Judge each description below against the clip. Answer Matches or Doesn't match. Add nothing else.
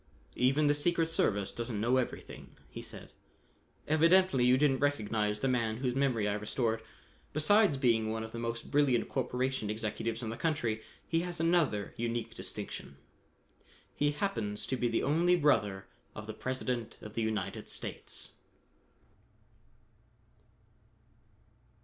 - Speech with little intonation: Doesn't match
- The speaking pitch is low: Matches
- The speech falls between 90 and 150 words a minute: Matches